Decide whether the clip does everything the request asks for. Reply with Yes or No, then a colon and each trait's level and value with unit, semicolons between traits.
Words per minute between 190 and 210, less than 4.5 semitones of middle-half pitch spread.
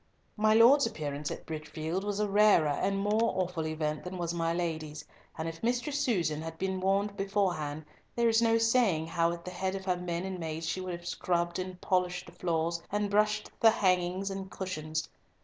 Yes: average, 200 wpm; average, 3.8 semitones